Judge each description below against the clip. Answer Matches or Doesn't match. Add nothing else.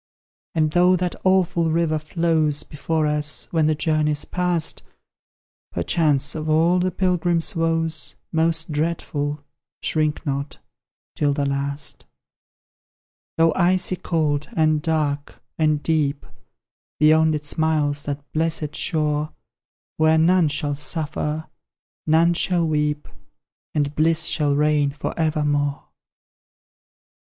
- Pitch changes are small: Matches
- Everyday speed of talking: Doesn't match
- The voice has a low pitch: Doesn't match